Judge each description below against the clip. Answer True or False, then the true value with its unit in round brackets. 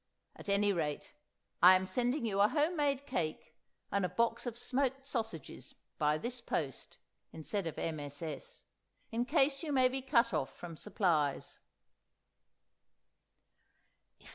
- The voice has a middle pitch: False (210 Hz)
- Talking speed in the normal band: False (130 wpm)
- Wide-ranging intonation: True (8.3 semitones)